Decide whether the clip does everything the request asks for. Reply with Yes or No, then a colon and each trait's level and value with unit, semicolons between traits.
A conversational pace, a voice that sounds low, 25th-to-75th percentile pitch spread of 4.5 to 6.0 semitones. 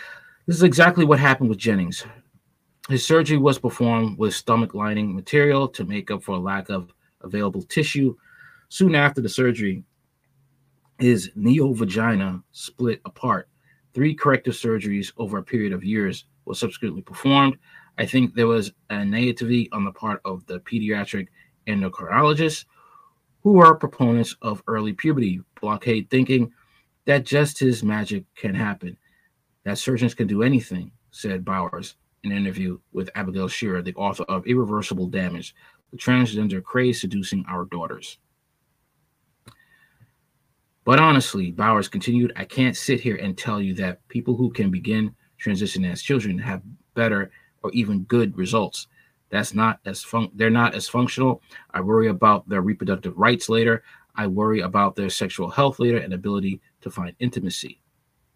Yes: average, 150 wpm; low, 115 Hz; average, 5.1 semitones